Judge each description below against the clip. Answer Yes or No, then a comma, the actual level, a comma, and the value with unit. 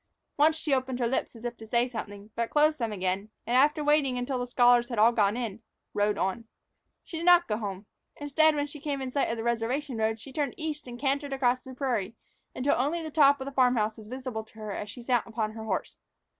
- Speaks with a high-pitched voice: Yes, high, 245 Hz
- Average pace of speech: No, fast, 245 wpm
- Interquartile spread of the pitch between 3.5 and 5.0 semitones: Yes, average, 4.2 semitones